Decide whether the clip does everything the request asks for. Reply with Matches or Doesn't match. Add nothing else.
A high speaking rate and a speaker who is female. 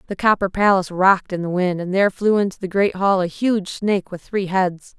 Matches